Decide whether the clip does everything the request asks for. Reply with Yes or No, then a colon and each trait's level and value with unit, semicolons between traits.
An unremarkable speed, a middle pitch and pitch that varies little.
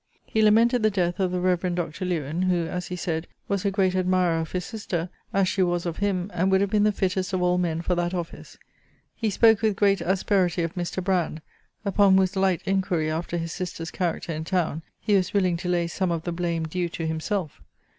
No: fast, 225 wpm; medium, 180 Hz; narrow, 2.2 semitones